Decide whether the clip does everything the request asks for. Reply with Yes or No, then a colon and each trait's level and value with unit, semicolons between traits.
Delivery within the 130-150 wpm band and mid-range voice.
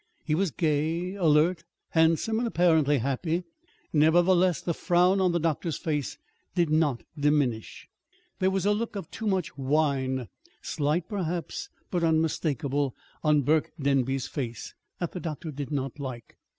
Yes: average, 145 wpm; medium, 160 Hz